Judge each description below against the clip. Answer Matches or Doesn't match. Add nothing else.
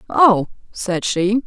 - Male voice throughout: Doesn't match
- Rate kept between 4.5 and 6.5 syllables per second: Doesn't match